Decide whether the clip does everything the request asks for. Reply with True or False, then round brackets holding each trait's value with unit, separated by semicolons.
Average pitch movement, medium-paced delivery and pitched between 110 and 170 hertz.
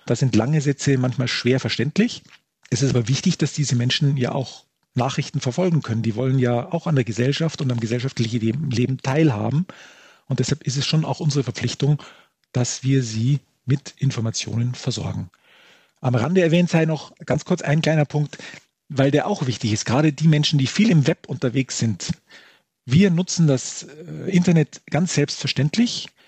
True (3.9 semitones; 170 wpm; 140 Hz)